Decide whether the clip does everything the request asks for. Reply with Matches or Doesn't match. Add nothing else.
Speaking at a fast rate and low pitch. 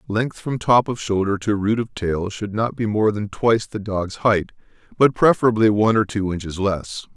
Matches